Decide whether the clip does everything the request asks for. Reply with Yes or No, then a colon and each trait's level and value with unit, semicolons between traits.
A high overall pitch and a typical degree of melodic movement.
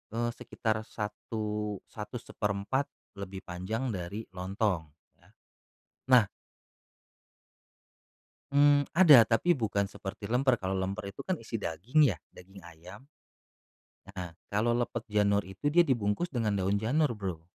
No: low, 105 Hz; average, 3.8 semitones